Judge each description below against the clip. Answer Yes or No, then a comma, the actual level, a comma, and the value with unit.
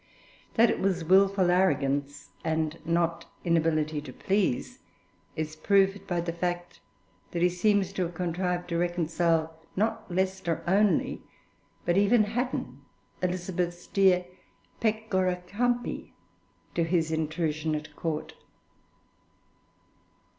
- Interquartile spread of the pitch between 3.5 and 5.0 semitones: No, average, 3.0 semitones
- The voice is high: No, medium, 175 Hz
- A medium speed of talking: No, slow, 110 wpm